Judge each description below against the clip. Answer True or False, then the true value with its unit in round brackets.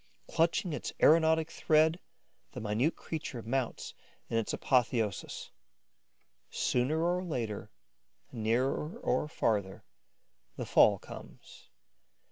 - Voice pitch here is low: True (130 Hz)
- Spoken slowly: True (95 wpm)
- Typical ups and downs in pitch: False (5.8 semitones)